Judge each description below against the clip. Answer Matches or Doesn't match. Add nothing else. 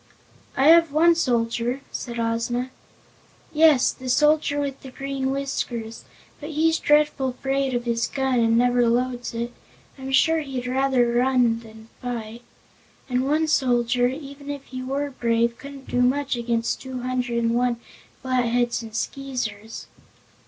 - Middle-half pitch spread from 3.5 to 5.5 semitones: Doesn't match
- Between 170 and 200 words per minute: Doesn't match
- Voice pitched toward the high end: Matches